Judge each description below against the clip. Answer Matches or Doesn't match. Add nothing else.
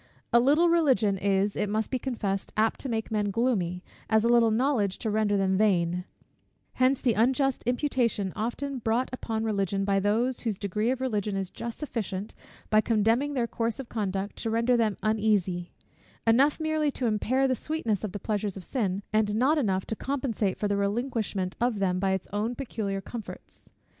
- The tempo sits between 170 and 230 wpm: Matches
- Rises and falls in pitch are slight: Doesn't match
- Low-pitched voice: Doesn't match